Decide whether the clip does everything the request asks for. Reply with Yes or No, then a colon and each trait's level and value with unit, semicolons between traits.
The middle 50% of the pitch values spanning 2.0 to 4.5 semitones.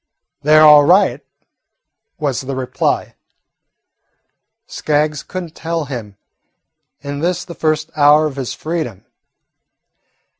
Yes: narrow, 2.6 semitones